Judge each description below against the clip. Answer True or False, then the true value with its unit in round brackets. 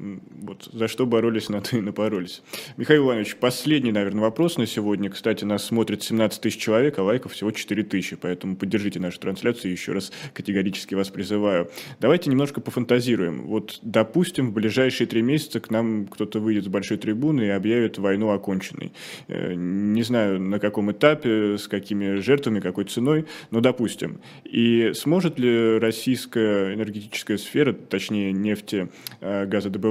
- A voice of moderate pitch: False (110 Hz)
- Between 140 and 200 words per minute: True (155 wpm)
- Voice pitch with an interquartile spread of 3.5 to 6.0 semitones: False (2.9 semitones)